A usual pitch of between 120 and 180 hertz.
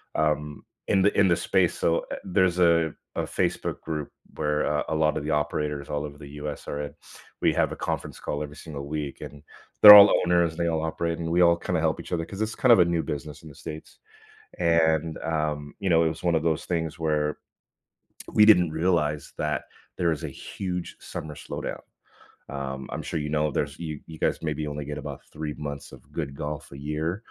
No: very low, 80 Hz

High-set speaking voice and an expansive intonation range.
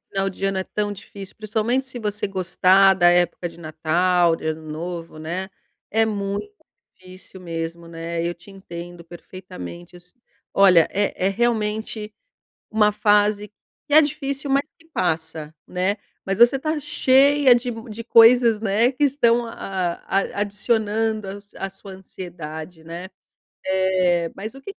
No: high, 195 Hz; average, 4.2 semitones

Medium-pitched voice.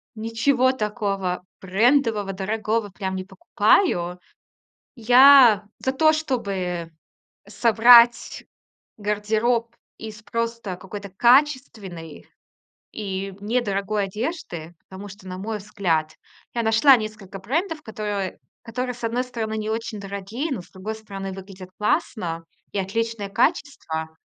No: high, 215 Hz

